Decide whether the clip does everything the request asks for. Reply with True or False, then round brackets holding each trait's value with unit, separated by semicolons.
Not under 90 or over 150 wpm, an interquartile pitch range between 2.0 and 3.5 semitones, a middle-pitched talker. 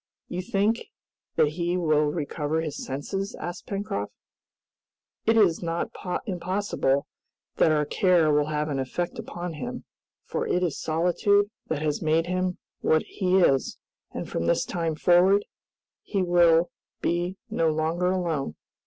True (145 wpm; 3.1 semitones; 175 Hz)